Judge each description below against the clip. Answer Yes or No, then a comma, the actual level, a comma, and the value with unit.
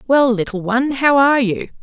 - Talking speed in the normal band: Yes, average, 195 wpm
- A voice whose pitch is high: Yes, high, 245 Hz